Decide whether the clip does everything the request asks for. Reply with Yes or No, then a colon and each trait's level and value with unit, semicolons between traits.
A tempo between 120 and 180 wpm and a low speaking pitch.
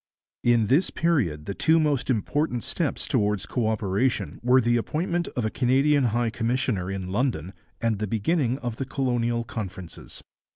Yes: average, 160 wpm; low, 120 Hz